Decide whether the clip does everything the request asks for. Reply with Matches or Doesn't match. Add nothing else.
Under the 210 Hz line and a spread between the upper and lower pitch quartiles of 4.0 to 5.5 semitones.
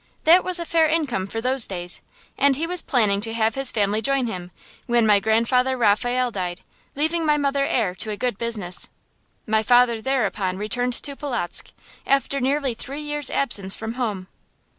Doesn't match